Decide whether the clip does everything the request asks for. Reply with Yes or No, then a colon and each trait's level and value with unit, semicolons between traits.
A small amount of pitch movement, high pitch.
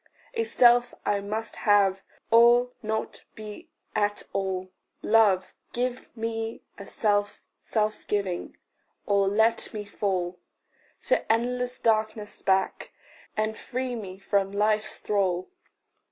Yes: narrow, 2.3 semitones; high, 215 Hz